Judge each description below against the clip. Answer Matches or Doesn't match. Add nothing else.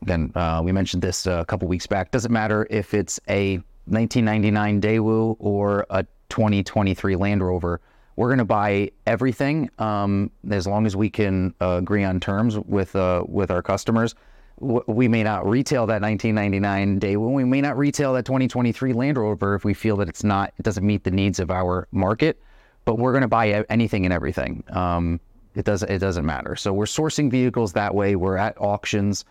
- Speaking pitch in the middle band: Doesn't match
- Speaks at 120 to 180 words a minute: Doesn't match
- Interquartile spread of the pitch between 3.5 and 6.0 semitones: Doesn't match